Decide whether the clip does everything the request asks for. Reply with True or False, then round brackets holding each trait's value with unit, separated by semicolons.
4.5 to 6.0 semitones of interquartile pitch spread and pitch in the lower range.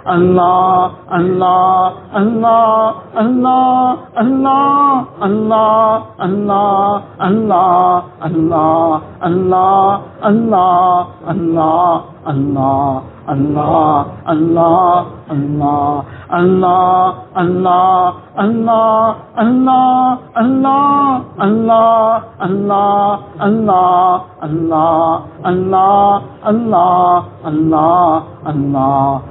False (5.2 semitones; 185 Hz)